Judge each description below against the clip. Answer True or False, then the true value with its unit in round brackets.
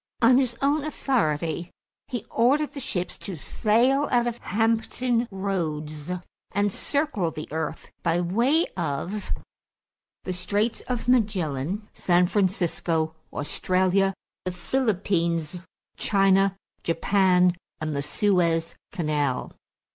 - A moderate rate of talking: False (110 wpm)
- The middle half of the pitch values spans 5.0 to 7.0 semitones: True (5.5 semitones)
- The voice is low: False (190 Hz)